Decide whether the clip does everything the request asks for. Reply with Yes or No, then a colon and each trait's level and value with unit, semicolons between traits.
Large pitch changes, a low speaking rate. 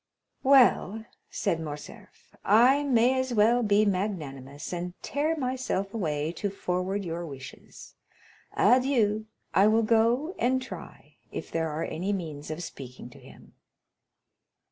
Yes: wide, 6.8 semitones; slow, 130 wpm